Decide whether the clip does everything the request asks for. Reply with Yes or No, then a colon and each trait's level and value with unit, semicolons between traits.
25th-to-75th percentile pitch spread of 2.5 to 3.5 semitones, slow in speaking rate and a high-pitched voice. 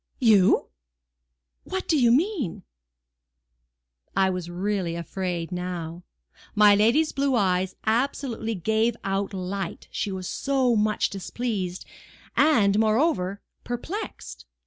No: average, 4.7 semitones; slow, 105 wpm; high, 210 Hz